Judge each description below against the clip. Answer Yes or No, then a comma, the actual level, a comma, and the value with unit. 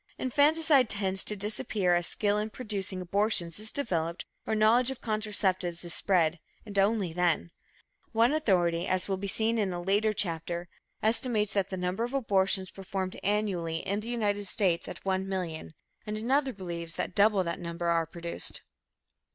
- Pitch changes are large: No, average, 3.6 semitones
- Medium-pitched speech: No, high, 195 Hz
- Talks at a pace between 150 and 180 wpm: Yes, average, 160 wpm